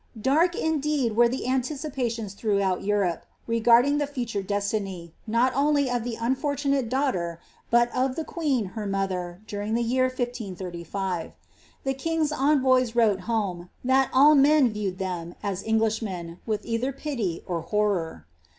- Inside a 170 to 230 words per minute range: No, average, 145 wpm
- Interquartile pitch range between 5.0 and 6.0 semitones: Yes, average, 5.3 semitones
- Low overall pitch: No, high, 230 Hz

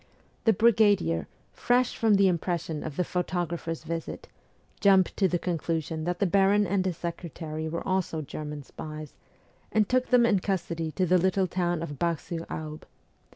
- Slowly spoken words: No, average, 170 wpm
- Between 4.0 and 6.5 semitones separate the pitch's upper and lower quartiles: No, average, 3.4 semitones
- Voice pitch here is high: No, medium, 175 Hz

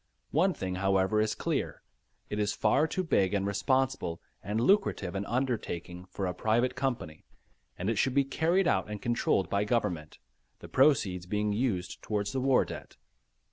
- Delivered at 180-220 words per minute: No, average, 170 wpm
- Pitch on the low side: Yes, low, 105 Hz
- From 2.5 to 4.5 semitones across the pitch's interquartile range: No, wide, 5.4 semitones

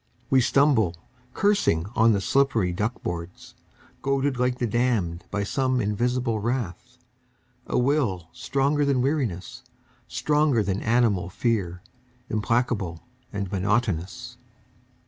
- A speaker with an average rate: No, slow, 110 wpm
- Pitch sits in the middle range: No, low, 115 Hz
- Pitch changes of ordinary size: Yes, average, 5.0 semitones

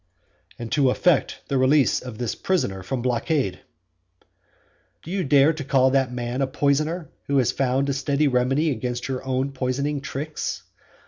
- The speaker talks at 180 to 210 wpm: No, average, 155 wpm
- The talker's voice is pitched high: No, low, 135 Hz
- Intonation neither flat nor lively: No, narrow, 2.3 semitones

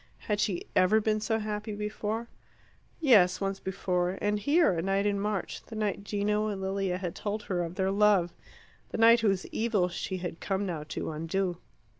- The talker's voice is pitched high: Yes, high, 200 Hz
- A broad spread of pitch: No, narrow, 2.4 semitones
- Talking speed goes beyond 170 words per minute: Yes, average, 185 wpm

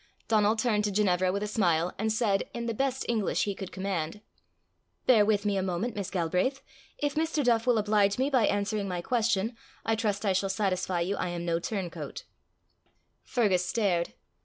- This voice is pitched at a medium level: No, high, 205 Hz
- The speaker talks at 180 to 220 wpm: Yes, average, 185 wpm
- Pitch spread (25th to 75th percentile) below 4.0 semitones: Yes, average, 3.4 semitones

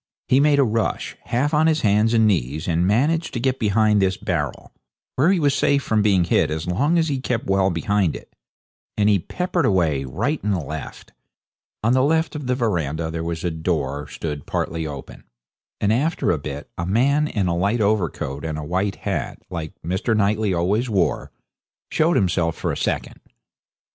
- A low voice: Yes, low, 100 Hz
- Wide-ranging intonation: Yes, wide, 7.2 semitones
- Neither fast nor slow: Yes, average, 190 wpm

